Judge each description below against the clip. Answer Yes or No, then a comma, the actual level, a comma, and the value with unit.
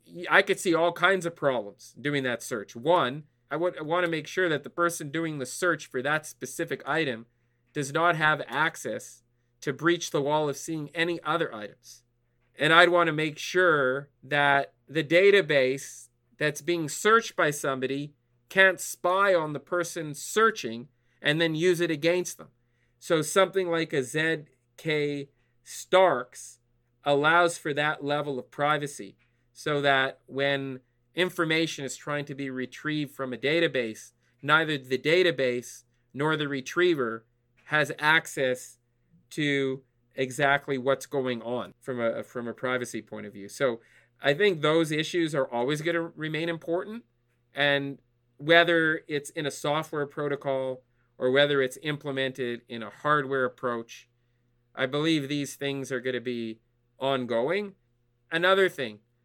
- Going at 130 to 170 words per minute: Yes, average, 150 wpm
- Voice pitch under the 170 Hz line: Yes, medium, 140 Hz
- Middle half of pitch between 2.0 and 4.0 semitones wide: No, average, 4.8 semitones